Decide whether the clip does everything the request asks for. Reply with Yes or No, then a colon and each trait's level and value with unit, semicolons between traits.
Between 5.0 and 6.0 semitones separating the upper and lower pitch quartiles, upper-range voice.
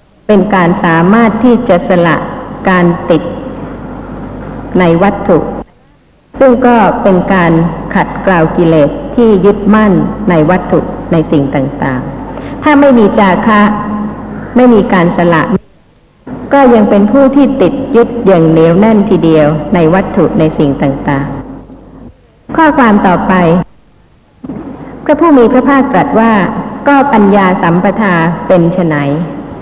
Yes: average, 5.3 semitones; high, 195 Hz